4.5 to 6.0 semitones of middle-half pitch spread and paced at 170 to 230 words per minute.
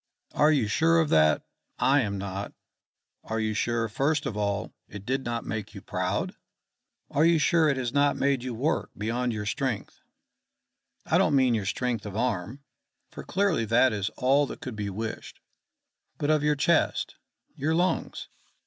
Yes: wide, 5.4 semitones; average, 175 wpm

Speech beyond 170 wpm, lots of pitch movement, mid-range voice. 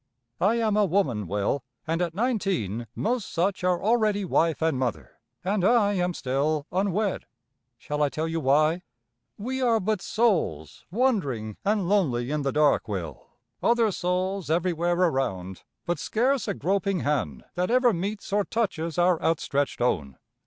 No: average, 155 wpm; wide, 6.3 semitones; medium, 175 Hz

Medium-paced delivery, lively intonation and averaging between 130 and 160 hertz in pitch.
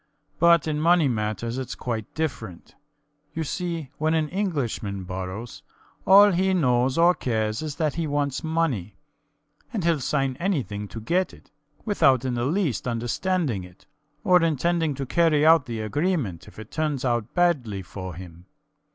Yes: average, 160 wpm; wide, 6.9 semitones; medium, 140 Hz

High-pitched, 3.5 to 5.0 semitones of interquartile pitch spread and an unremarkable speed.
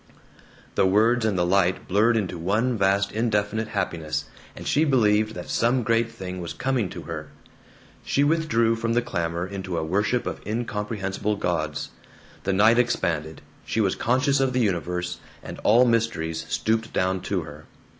No: low, 105 Hz; average, 4.1 semitones; average, 165 wpm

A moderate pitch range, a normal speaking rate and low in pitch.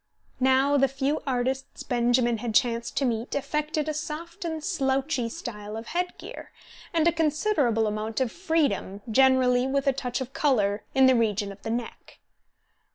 No: average, 4.3 semitones; average, 165 wpm; very high, 260 Hz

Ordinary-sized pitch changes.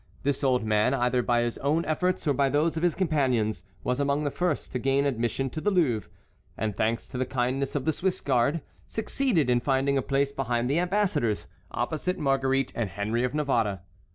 Yes: average, 3.8 semitones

